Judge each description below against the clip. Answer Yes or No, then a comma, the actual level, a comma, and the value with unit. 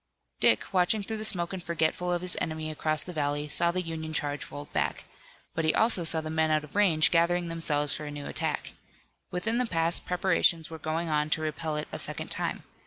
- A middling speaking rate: No, fast, 220 wpm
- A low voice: No, medium, 165 Hz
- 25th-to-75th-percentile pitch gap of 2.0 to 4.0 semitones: Yes, narrow, 2.4 semitones